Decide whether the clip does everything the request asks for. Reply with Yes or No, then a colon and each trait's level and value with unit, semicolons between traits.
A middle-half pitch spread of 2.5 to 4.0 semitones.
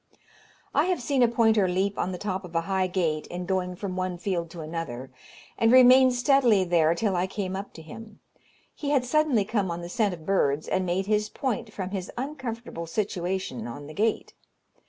No: average, 4.5 semitones